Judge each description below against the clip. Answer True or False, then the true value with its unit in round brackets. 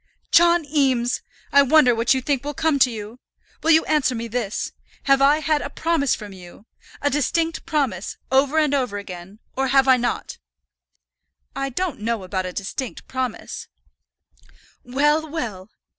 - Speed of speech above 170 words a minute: False (165 wpm)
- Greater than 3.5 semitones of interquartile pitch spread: True (4.5 semitones)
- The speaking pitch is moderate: False (265 Hz)